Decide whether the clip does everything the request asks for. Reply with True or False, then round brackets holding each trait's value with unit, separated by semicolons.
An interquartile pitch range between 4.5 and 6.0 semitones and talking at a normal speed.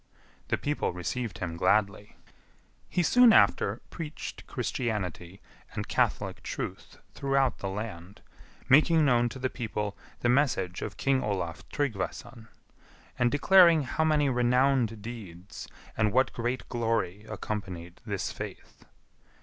False (5.3 semitones; 125 wpm)